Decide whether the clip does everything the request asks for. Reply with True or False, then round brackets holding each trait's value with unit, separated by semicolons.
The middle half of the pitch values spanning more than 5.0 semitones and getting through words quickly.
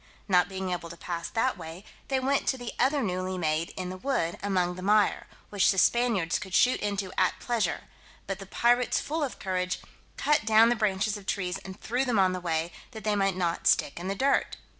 False (4.3 semitones; 220 wpm)